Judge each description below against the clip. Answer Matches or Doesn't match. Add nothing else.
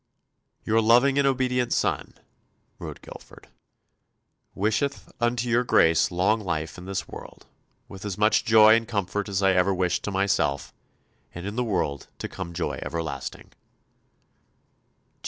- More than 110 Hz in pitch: Doesn't match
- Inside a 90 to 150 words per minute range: Matches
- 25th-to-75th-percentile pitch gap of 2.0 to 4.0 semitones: Doesn't match